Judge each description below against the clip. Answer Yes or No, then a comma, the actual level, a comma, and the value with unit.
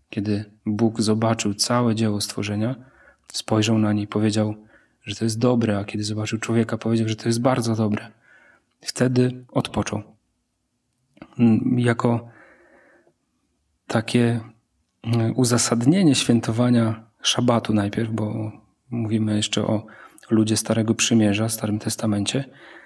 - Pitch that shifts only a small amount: Yes, narrow, 1.7 semitones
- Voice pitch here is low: Yes, low, 110 Hz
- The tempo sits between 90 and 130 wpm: Yes, slow, 110 wpm